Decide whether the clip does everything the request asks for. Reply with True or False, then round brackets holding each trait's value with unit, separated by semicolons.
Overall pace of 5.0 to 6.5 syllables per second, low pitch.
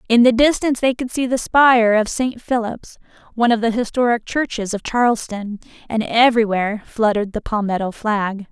False (5.5 syllables/s; 230 Hz)